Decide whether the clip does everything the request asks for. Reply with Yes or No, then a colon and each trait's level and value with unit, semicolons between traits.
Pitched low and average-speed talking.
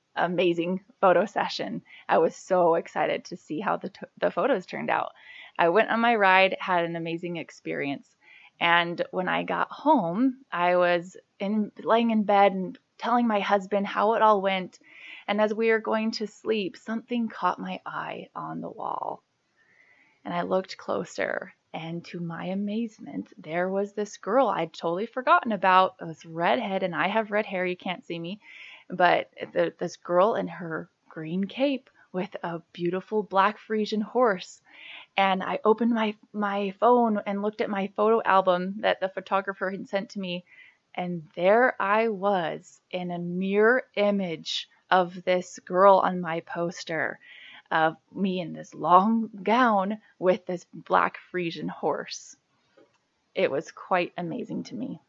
No: high, 195 Hz; average, 165 wpm